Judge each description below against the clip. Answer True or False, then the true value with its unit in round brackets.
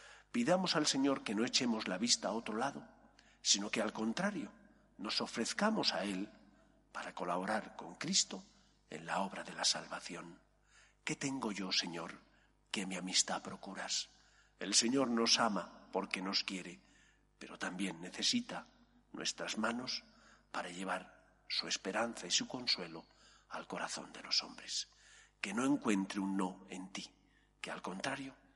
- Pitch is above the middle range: False (115 Hz)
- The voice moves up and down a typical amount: False (6.8 semitones)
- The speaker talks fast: False (150 wpm)